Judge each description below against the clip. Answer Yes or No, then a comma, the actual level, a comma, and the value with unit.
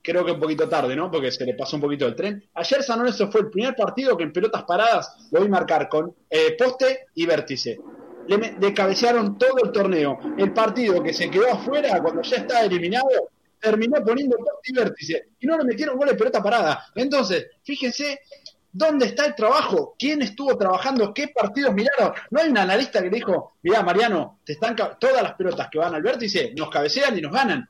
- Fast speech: Yes, fast, 205 wpm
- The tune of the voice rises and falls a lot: Yes, wide, 6.5 semitones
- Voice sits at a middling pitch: No, high, 235 Hz